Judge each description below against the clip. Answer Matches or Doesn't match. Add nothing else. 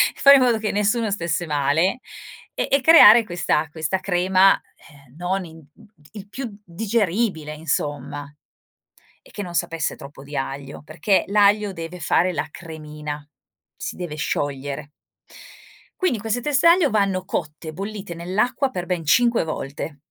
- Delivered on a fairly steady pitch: Doesn't match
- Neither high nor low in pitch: Matches